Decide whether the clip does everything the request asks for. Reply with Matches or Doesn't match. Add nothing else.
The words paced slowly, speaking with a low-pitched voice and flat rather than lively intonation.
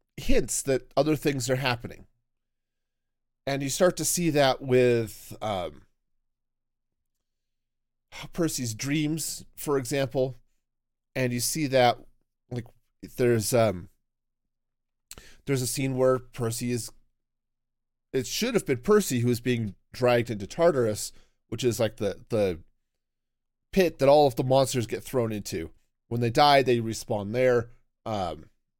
Matches